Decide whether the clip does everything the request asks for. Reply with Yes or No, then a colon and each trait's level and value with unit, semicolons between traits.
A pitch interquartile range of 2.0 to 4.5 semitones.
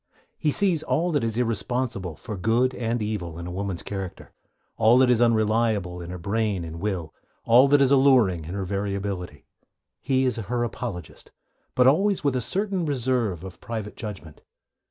No: average, 5.2 semitones